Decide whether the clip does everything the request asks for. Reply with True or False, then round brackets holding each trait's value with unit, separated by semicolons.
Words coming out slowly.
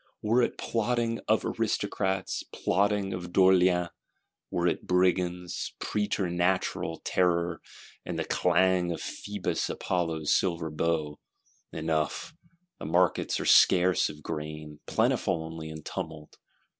True (110 wpm)